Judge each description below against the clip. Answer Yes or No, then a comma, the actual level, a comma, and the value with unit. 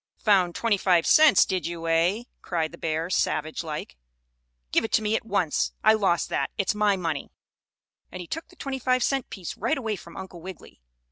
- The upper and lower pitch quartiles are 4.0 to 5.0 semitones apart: Yes, average, 4.7 semitones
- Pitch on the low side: No, high, 190 Hz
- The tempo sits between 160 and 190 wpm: No, average, 200 wpm